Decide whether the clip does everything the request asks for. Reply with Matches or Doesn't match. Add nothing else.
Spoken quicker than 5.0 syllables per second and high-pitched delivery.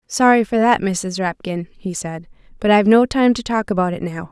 Matches